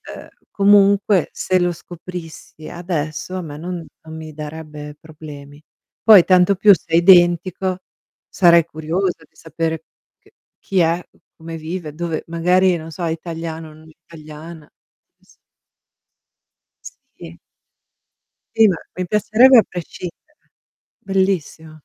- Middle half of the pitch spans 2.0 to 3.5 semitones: Yes, average, 2.7 semitones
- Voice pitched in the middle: Yes, medium, 170 Hz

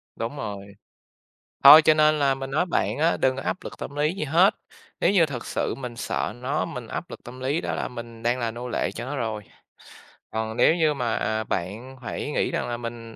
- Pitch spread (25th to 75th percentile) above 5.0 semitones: No, average, 4.3 semitones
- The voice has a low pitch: Yes, low, 125 Hz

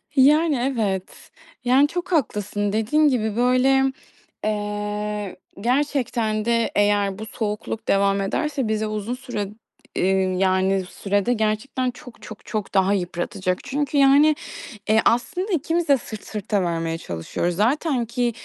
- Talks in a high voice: Yes, high, 220 Hz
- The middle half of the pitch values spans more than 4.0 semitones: Yes, average, 4.7 semitones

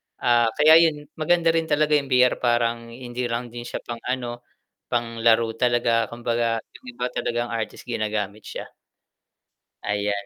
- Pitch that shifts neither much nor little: No, narrow, 1.6 semitones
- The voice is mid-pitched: No, low, 120 Hz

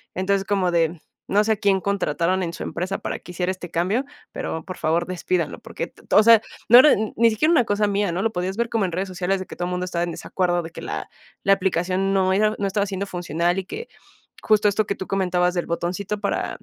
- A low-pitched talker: No, high, 190 Hz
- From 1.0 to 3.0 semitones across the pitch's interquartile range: Yes, narrow, 2.5 semitones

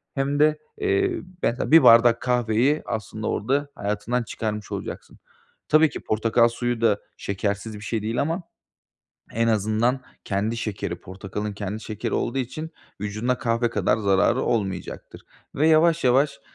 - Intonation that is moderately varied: Yes, average, 4.3 semitones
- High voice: No, low, 115 Hz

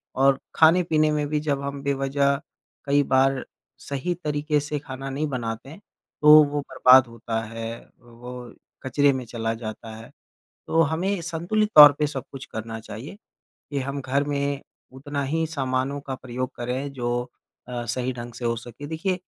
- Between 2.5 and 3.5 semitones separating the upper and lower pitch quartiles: Yes, average, 3.2 semitones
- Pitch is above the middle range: No, low, 135 Hz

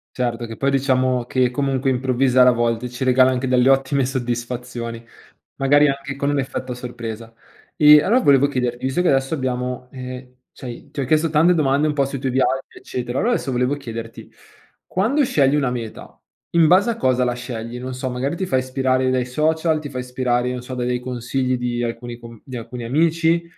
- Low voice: Yes, low, 130 Hz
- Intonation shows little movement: Yes, narrow, 2.1 semitones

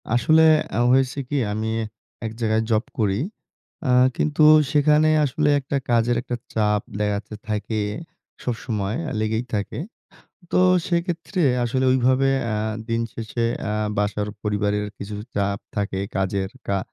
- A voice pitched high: No, low, 110 Hz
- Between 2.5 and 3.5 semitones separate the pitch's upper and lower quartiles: No, average, 4.1 semitones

